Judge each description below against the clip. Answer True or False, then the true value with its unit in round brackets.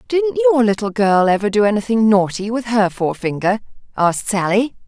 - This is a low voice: False (220 Hz)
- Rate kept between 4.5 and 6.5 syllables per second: True (5.4 syllables/s)